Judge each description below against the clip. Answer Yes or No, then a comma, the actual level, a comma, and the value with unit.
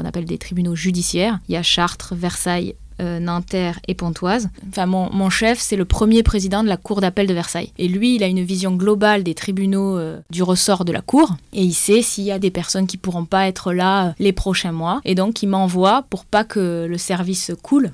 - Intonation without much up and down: Yes, narrow, 2.0 semitones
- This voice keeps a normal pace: No, fast, 235 wpm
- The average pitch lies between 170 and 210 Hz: Yes, medium, 185 Hz